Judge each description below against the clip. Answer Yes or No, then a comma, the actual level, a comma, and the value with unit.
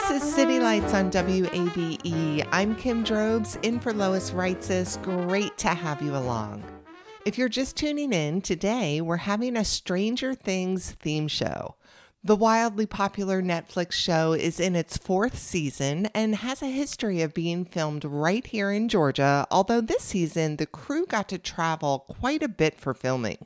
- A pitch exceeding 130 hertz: Yes, medium, 185 Hz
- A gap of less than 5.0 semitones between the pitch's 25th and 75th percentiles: No, wide, 5.4 semitones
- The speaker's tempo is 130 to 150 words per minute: No, average, 165 wpm